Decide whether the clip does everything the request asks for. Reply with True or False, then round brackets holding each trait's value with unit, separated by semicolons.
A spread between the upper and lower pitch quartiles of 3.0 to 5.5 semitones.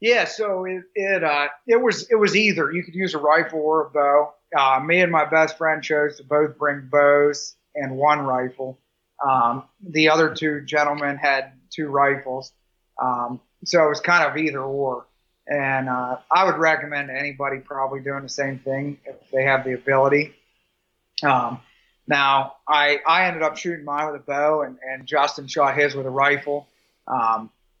False (2.5 semitones)